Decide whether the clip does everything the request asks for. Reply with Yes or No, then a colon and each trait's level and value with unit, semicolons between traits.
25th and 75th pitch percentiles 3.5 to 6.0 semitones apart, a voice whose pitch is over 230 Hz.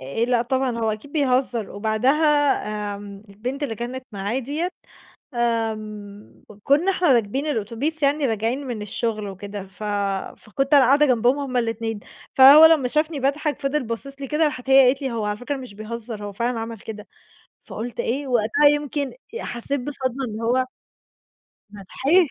Yes: average, 4.3 semitones; high, 245 Hz